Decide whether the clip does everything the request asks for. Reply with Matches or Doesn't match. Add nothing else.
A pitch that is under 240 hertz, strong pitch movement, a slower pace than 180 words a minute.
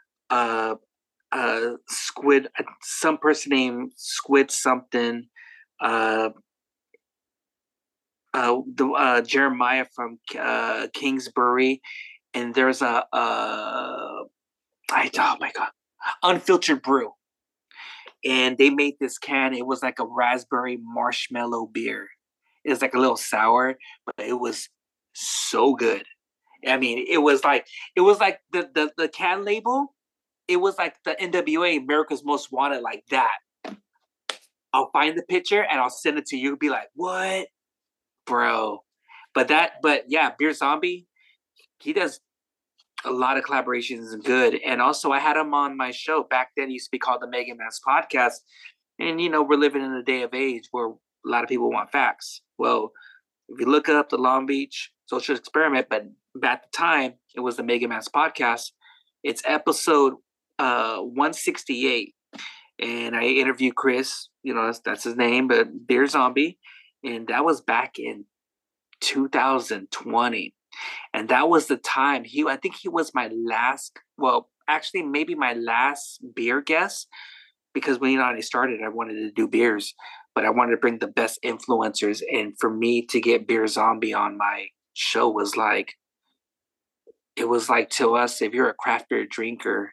Matches